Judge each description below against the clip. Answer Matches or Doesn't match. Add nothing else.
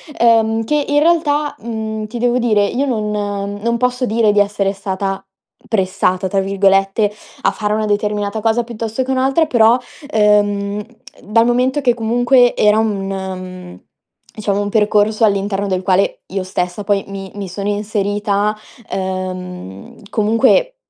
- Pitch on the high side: Matches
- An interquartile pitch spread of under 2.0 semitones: Doesn't match